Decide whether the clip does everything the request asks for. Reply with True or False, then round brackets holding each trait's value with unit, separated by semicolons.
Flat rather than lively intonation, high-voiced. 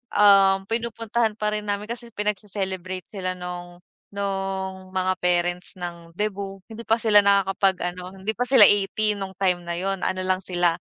True (2.2 semitones; 195 Hz)